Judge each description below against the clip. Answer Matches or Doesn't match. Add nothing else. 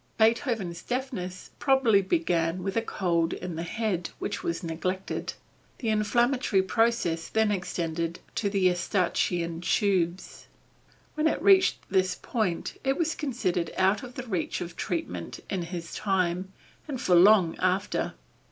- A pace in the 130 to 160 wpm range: Matches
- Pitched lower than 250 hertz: Matches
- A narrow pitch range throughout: Doesn't match